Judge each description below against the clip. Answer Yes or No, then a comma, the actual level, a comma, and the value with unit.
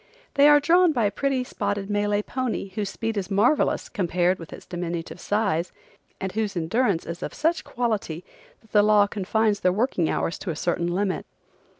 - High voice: Yes, high, 205 Hz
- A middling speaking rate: Yes, average, 185 wpm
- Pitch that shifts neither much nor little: Yes, average, 3.8 semitones